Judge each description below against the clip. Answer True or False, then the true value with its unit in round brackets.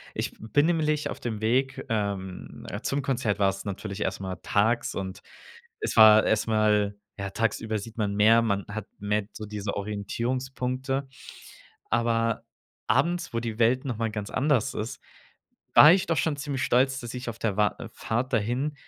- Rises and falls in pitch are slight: False (3.7 semitones)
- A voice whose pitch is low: True (115 Hz)